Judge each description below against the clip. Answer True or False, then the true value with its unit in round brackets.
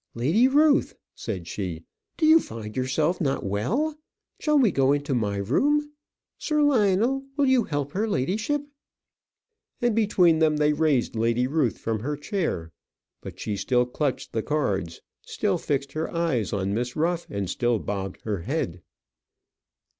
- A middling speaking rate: True (155 wpm)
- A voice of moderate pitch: True (145 Hz)